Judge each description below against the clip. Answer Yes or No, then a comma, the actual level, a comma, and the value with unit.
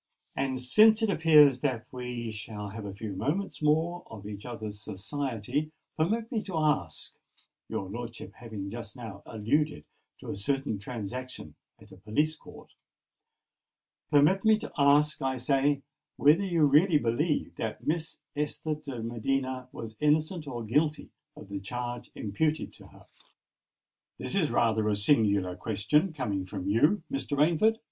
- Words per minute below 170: Yes, average, 145 wpm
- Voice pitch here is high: No, low, 130 Hz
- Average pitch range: No, wide, 5.9 semitones